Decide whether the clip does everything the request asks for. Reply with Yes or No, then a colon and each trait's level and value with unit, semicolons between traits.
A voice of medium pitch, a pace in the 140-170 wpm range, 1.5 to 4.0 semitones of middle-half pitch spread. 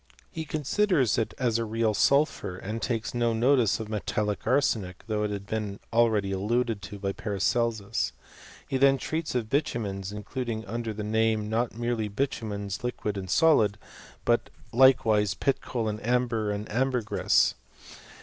No: low, 110 Hz; average, 150 wpm; average, 3.1 semitones